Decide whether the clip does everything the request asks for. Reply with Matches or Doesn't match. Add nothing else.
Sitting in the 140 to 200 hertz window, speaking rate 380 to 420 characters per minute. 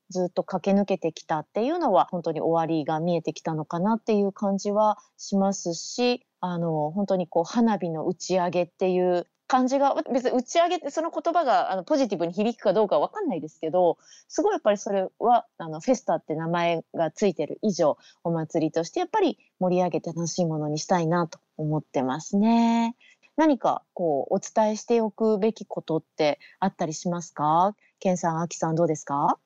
Matches